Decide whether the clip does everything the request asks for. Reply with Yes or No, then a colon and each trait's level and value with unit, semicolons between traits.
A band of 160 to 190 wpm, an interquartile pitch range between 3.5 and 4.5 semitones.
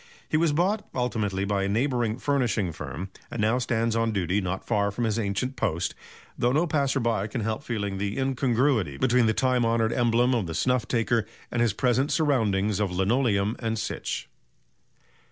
Yes: average, 180 wpm; average, 3.8 semitones